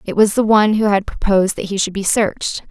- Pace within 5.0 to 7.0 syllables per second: Yes, 6.3 syllables/s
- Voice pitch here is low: No, high, 205 Hz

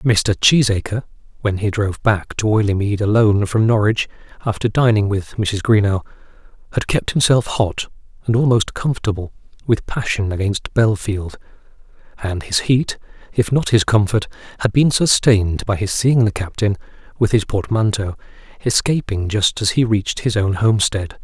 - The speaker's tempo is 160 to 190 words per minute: No, average, 150 wpm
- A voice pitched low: Yes, low, 105 Hz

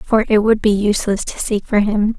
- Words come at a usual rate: No, fast, 245 wpm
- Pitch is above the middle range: Yes, high, 210 Hz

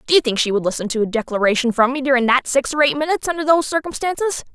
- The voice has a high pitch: Yes, very high, 270 Hz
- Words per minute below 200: No, fast, 265 wpm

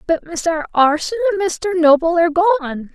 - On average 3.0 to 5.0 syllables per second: No, 5.5 syllables/s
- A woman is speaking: Yes, female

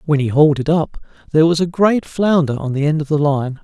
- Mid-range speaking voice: Yes, medium, 155 Hz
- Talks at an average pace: No, fast, 265 wpm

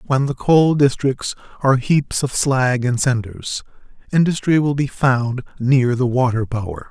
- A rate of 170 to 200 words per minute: No, average, 155 wpm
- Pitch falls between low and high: No, low, 130 Hz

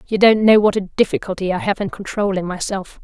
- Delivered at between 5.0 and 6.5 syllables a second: Yes, 6.0 syllables/s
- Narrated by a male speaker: No, female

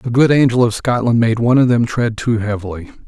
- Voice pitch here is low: Yes, low, 115 Hz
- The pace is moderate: No, fast, 235 wpm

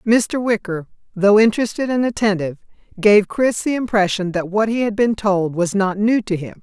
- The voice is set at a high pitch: Yes, high, 210 Hz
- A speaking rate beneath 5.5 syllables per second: Yes, 5.2 syllables/s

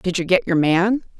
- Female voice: Yes, female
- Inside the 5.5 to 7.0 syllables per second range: No, 4.8 syllables/s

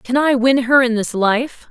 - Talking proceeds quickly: Yes, fast, 245 wpm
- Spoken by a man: No, female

